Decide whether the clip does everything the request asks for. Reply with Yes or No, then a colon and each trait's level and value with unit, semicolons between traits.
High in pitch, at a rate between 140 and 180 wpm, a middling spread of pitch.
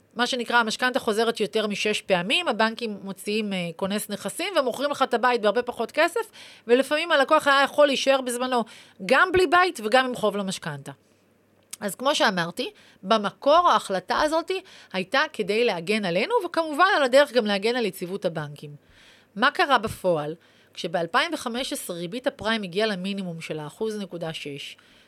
No: high, 230 Hz; average, 145 wpm; wide, 5.9 semitones